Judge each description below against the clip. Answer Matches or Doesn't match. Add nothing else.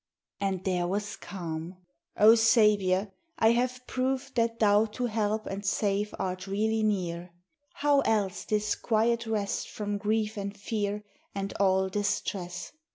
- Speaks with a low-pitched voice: Doesn't match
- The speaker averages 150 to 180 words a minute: Doesn't match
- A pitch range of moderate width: Doesn't match